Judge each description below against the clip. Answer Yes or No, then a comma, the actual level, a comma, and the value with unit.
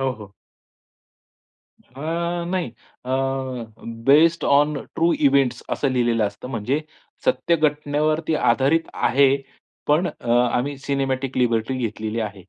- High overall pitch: No, low, 135 Hz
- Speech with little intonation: No, average, 4.0 semitones